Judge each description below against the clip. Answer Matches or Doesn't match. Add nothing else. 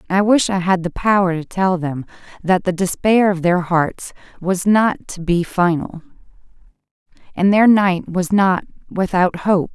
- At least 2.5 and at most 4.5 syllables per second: Matches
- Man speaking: Doesn't match